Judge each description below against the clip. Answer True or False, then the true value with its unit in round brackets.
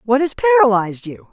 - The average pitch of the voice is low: False (250 Hz)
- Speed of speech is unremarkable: True (180 wpm)